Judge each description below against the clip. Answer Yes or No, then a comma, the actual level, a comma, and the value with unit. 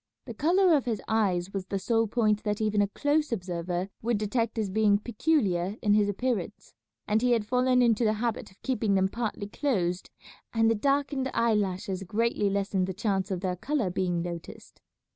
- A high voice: Yes, high, 210 Hz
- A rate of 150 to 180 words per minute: No, average, 190 wpm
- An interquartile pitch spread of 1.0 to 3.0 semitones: No, average, 3.6 semitones